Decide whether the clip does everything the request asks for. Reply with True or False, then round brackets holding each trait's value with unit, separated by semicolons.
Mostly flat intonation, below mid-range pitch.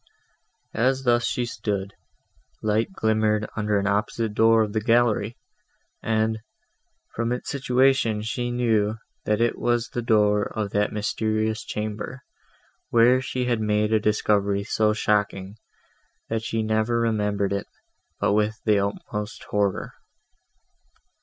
True (1.9 semitones; 110 Hz)